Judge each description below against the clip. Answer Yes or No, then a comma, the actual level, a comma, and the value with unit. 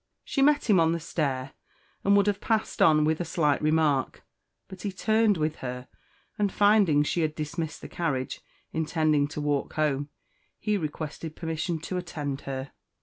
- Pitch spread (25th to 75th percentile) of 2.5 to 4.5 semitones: Yes, average, 3.9 semitones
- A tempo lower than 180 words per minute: Yes, average, 170 wpm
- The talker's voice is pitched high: No, medium, 160 Hz